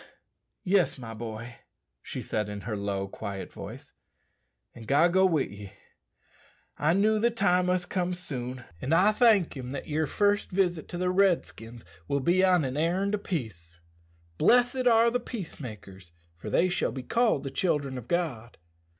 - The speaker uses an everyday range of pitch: No, wide, 8.1 semitones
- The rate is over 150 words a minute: Yes, average, 175 wpm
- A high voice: No, medium, 160 Hz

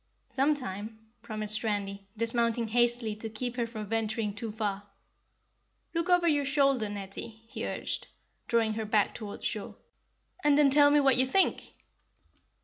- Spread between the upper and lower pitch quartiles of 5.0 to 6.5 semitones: No, average, 3.8 semitones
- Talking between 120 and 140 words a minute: No, average, 150 wpm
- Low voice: No, high, 225 Hz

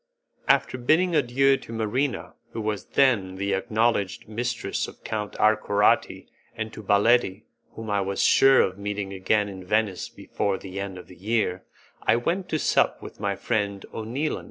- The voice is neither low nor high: No, low, 105 Hz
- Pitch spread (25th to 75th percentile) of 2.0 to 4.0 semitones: Yes, average, 3.4 semitones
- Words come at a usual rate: Yes, average, 165 wpm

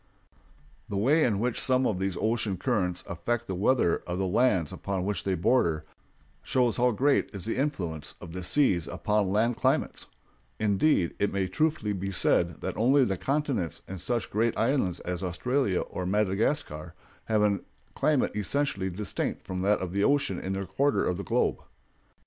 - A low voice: Yes, low, 100 Hz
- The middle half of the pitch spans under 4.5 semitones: No, average, 5.0 semitones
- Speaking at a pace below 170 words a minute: No, average, 175 wpm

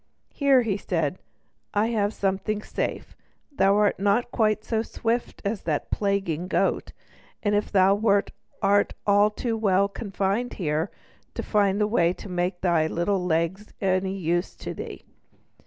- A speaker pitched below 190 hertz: No, high, 200 Hz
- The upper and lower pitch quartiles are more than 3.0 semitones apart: No, average, 2.7 semitones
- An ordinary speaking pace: Yes, average, 150 wpm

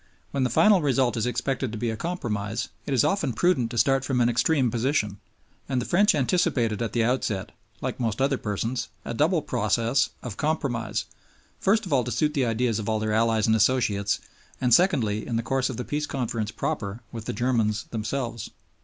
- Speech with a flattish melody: No, average, 3.4 semitones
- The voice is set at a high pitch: No, low, 120 Hz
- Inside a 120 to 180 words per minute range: No, average, 195 wpm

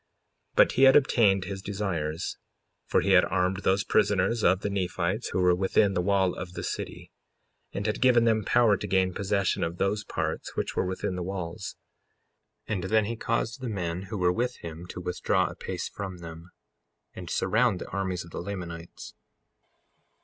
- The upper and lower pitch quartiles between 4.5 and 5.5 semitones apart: No, average, 2.7 semitones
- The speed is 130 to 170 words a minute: No, average, 190 wpm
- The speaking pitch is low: Yes, very low, 95 Hz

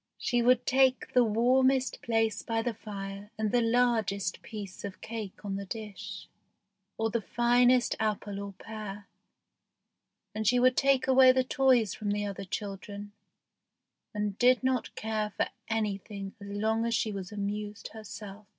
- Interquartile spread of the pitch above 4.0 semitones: No, average, 3.1 semitones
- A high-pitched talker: Yes, high, 220 Hz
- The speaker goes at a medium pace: Yes, average, 155 wpm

